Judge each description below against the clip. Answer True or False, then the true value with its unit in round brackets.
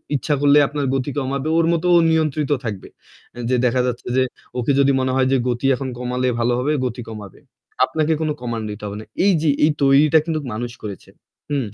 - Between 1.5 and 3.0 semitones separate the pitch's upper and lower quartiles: False (3.5 semitones)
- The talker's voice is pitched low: True (130 Hz)